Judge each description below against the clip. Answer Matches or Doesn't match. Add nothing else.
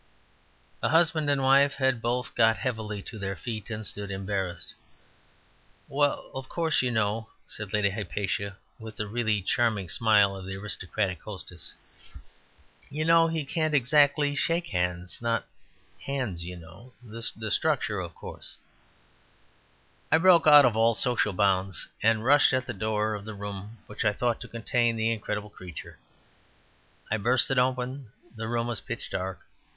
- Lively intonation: Doesn't match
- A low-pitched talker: Matches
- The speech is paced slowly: Doesn't match